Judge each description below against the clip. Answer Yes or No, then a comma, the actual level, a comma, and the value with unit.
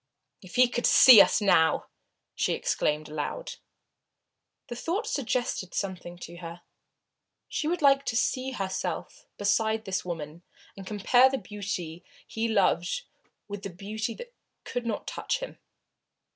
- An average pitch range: No, wide, 5.8 semitones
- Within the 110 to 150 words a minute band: Yes, average, 145 wpm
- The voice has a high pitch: Yes, high, 205 Hz